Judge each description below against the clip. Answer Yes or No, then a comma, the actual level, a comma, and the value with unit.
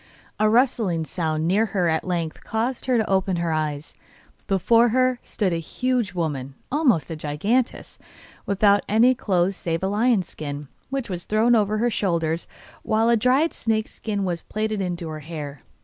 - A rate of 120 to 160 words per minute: No, average, 170 wpm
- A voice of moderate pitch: No, high, 195 Hz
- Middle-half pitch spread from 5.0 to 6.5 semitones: Yes, wide, 5.6 semitones